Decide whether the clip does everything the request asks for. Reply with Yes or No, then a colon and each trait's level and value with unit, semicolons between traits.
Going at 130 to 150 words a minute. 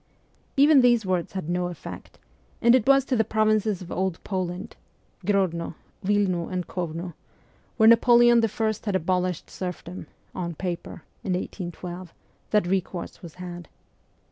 Yes: average, 140 wpm